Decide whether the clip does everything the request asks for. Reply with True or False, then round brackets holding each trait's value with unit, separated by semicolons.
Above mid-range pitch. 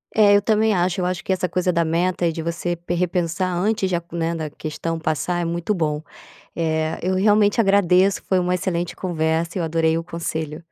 False (175 Hz)